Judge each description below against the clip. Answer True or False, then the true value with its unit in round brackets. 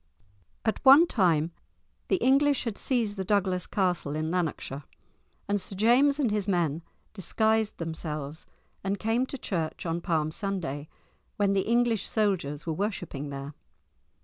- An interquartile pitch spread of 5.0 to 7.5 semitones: True (5.5 semitones)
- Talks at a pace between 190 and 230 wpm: False (145 wpm)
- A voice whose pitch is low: False (195 Hz)